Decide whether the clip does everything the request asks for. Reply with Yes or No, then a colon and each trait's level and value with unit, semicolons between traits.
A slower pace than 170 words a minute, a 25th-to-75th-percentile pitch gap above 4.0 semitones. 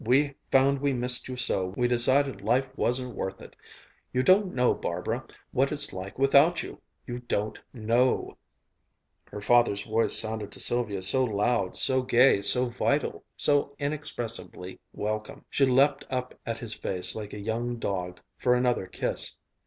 No: average, 160 wpm; average, 3.6 semitones